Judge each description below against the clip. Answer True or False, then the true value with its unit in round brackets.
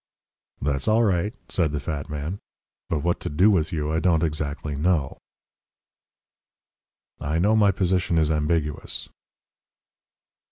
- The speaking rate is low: True (130 wpm)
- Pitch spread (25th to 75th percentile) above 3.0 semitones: True (3.5 semitones)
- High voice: False (80 Hz)